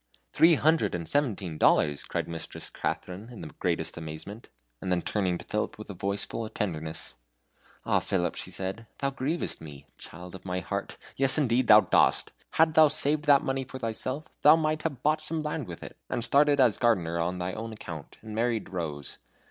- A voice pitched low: Yes, low, 110 Hz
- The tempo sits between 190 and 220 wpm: Yes, average, 195 wpm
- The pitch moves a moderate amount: No, wide, 7.9 semitones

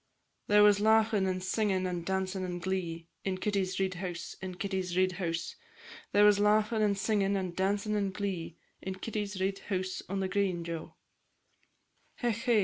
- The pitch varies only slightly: Yes, narrow, 1.9 semitones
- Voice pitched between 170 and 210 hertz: Yes, high, 190 Hz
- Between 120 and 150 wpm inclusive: No, average, 170 wpm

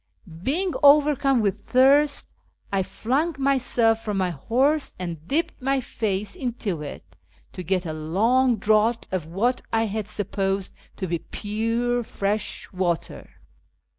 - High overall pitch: Yes, high, 220 Hz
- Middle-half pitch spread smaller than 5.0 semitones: No, wide, 5.4 semitones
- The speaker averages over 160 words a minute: No, slow, 135 wpm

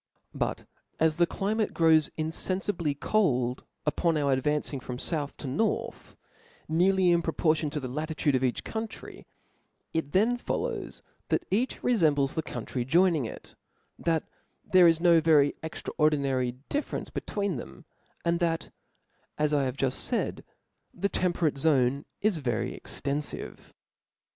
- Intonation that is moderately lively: Yes, average, 4.0 semitones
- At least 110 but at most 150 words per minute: Yes, average, 145 wpm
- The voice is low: No, medium, 155 Hz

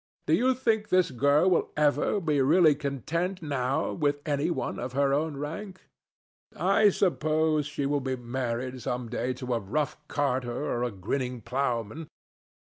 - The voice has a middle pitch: Yes, medium, 145 Hz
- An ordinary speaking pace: Yes, average, 160 wpm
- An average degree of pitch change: Yes, average, 4.0 semitones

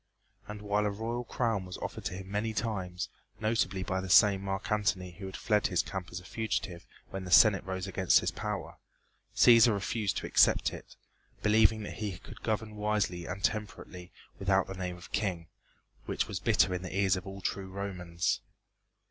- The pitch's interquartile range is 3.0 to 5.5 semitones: No, narrow, 2.4 semitones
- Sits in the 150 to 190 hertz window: No, very low, 95 Hz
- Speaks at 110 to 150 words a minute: No, average, 190 wpm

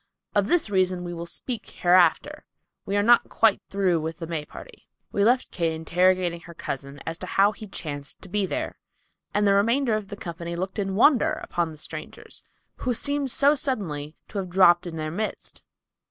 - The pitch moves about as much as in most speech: Yes, average, 4.1 semitones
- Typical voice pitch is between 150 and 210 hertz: Yes, medium, 185 Hz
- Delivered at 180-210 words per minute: Yes, average, 195 wpm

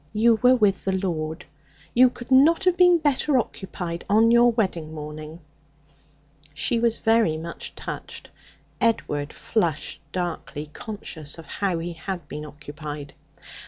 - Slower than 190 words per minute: Yes, slow, 135 wpm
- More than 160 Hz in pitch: Yes, medium, 185 Hz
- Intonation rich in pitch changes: Yes, wide, 7.0 semitones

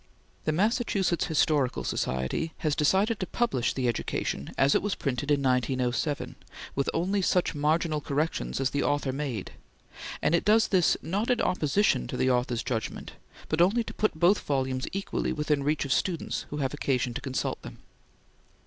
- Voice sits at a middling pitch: Yes, medium, 145 Hz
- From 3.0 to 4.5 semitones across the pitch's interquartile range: No, average, 5.1 semitones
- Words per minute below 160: No, average, 165 wpm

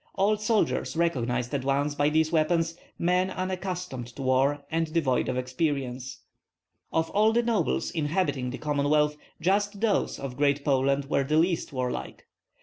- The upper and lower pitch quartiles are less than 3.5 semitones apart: No, average, 4.8 semitones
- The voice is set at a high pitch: No, medium, 150 Hz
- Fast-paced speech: No, average, 150 wpm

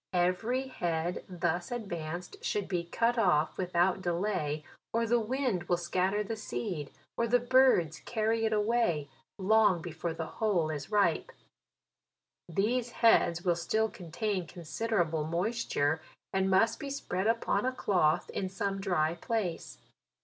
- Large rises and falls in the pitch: No, average, 4.7 semitones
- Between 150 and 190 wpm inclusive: No, average, 140 wpm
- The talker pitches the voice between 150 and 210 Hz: Yes, high, 190 Hz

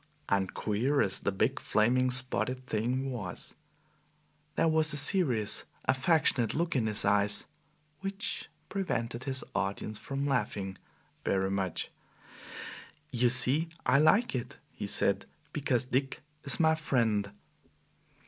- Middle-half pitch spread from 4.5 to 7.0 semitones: Yes, average, 5.1 semitones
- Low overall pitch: Yes, low, 125 Hz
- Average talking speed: No, slow, 125 wpm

